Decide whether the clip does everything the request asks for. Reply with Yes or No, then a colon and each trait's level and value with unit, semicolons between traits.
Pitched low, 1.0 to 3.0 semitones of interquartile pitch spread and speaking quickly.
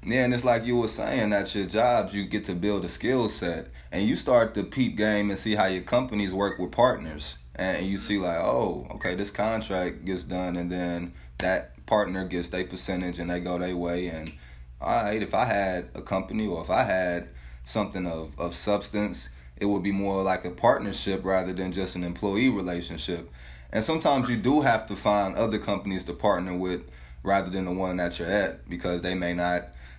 Yes: very low, 90 Hz; narrow, 2.5 semitones; fast, 210 wpm